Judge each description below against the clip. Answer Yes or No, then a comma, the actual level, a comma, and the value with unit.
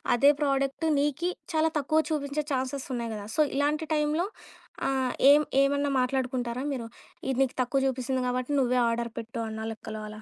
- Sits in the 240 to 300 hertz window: Yes, very high, 265 Hz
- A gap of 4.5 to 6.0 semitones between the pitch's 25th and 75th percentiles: No, average, 2.8 semitones